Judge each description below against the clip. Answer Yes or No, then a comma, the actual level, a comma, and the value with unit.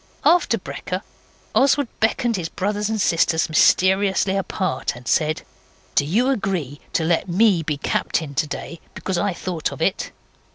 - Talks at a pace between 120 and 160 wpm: Yes, average, 150 wpm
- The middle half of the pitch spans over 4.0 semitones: Yes, average, 4.5 semitones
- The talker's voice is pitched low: No, medium, 185 Hz